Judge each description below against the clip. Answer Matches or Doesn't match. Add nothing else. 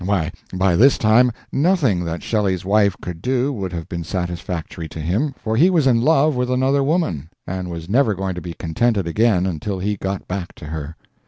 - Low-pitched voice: Matches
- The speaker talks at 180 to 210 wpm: Matches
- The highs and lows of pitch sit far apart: Matches